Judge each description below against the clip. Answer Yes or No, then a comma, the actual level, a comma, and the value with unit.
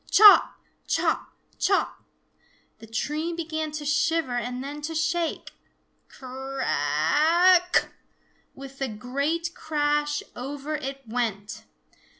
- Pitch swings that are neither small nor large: Yes, average, 3.9 semitones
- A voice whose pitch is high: Yes, very high, 290 Hz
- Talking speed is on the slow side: Yes, slow, 110 wpm